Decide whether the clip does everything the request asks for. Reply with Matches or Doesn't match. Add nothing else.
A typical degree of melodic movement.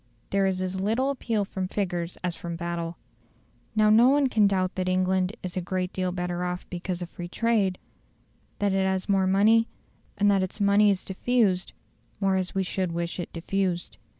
Doesn't match